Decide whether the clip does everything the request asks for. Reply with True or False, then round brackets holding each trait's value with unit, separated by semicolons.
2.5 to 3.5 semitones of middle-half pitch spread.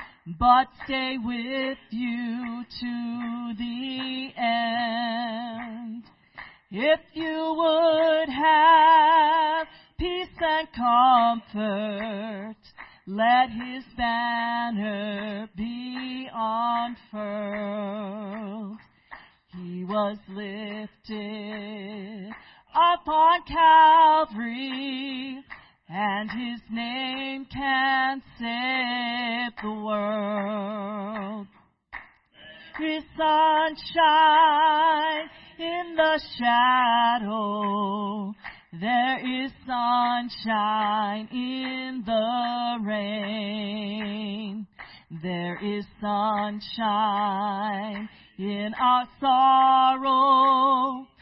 False (4.0 semitones)